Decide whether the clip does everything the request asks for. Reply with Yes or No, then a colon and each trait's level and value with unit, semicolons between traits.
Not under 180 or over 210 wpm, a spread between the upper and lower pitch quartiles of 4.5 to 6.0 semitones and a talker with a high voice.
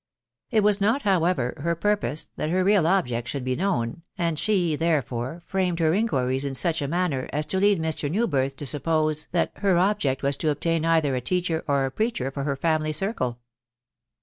No: average, 195 wpm; average, 5.0 semitones; medium, 160 Hz